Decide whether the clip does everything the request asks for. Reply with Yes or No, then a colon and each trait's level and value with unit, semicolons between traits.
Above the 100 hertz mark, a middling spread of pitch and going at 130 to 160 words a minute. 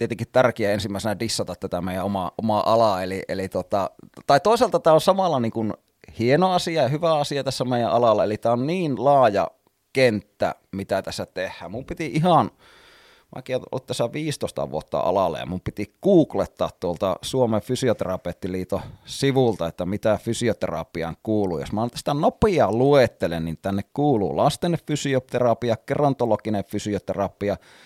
No: low, 120 Hz; wide, 6.2 semitones; average, 145 wpm